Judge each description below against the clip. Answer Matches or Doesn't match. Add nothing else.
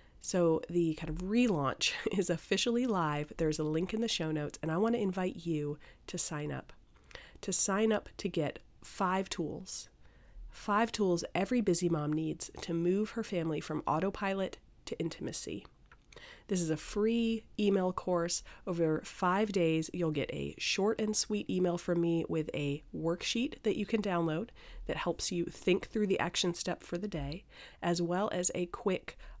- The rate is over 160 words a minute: Matches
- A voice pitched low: Doesn't match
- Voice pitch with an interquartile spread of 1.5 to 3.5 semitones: Doesn't match